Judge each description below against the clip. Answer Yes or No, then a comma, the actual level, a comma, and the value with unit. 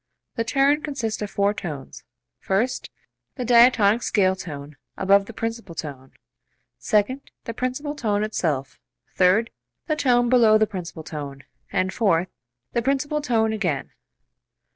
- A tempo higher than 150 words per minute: No, slow, 135 wpm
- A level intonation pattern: No, average, 5.2 semitones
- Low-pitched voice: No, high, 215 Hz